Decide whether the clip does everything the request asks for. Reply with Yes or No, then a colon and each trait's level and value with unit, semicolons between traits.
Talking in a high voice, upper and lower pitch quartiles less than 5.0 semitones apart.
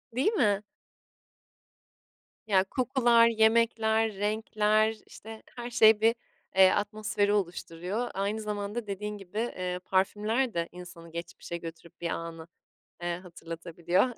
Yes: high, 210 Hz; average, 3.8 semitones